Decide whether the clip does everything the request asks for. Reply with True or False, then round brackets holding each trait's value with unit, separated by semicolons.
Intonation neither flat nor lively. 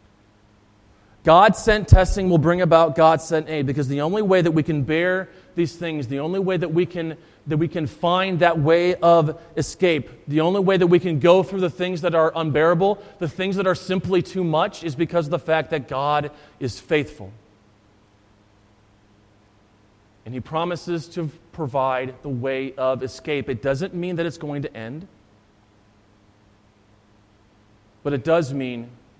False (8.1 semitones)